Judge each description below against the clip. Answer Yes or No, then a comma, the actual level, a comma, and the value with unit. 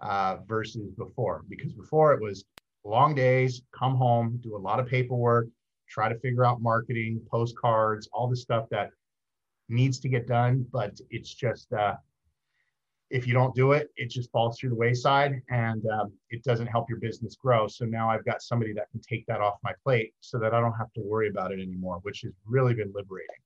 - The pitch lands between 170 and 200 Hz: No, low, 115 Hz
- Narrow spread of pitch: Yes, narrow, 2.3 semitones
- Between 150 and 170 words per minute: No, fast, 205 wpm